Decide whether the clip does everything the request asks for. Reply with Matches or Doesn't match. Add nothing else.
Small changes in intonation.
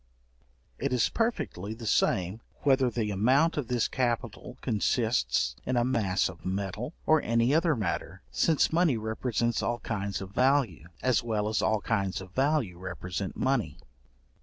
Doesn't match